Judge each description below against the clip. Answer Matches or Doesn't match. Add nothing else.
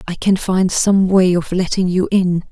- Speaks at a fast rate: Matches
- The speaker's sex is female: Matches